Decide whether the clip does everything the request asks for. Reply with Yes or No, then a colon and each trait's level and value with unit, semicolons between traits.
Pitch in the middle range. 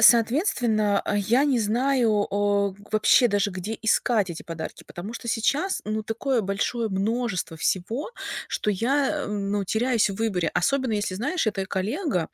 No: high, 215 Hz